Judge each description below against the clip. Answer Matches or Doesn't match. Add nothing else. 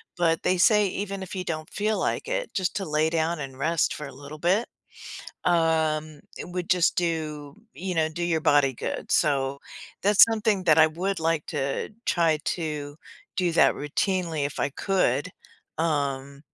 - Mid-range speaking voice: Matches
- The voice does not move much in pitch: Doesn't match